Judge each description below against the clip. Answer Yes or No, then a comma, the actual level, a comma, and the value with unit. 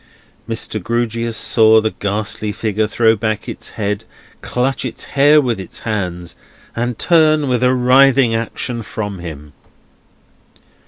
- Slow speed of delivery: Yes, slow, 130 wpm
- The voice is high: No, low, 115 Hz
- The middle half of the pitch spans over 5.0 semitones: No, average, 3.1 semitones